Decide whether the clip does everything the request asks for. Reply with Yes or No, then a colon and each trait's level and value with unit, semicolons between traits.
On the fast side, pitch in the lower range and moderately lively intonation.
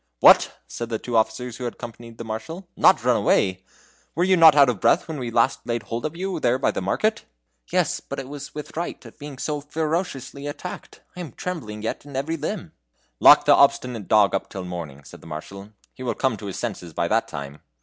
No: fast, 230 wpm; low, 120 Hz; wide, 5.9 semitones